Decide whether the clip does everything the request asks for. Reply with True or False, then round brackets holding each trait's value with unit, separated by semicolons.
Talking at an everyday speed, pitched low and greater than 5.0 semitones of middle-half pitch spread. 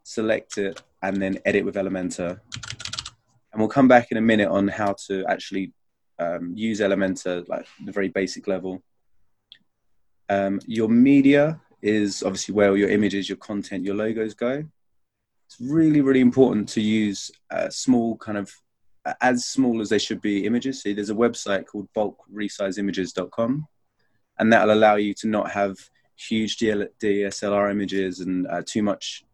False (165 wpm; 105 Hz; 2.8 semitones)